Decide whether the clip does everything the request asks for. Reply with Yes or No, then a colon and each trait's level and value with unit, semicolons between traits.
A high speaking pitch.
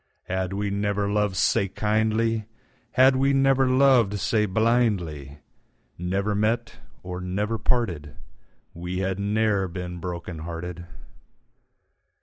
No: low, 100 Hz